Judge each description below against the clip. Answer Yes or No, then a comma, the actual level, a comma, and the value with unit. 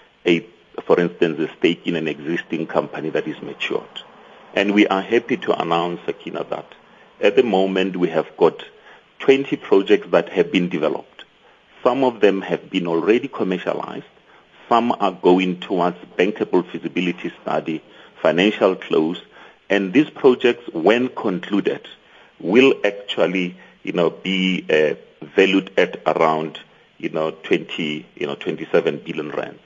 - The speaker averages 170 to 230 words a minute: No, average, 140 wpm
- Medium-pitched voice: No, very low, 90 Hz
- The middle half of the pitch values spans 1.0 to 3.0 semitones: Yes, narrow, 2.6 semitones